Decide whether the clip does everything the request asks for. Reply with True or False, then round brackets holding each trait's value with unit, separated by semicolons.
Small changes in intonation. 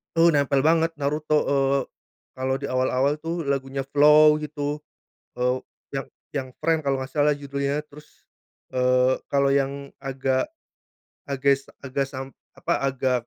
True (1.9 semitones)